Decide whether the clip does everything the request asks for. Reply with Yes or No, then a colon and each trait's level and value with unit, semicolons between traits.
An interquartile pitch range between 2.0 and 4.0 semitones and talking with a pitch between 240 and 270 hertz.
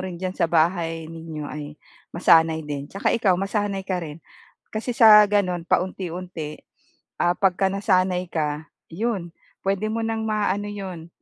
No: average, 3.4 semitones; medium, 185 Hz